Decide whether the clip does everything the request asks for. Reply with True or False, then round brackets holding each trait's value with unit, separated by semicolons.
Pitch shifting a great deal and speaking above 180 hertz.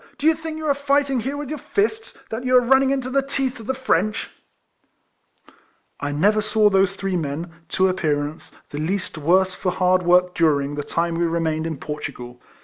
True (8.3 semitones; 190 Hz)